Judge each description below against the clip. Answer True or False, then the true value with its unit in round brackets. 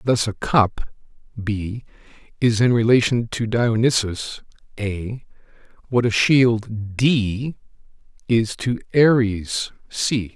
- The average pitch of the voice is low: True (115 Hz)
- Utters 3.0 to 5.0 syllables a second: True (4.1 syllables/s)